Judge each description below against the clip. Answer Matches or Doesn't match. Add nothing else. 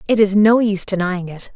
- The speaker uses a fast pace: Matches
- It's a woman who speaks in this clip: Matches